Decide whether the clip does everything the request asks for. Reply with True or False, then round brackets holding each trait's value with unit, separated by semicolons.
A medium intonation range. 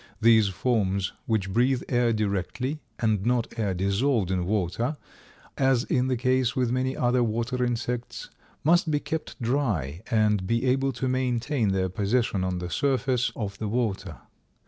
True (4.3 semitones)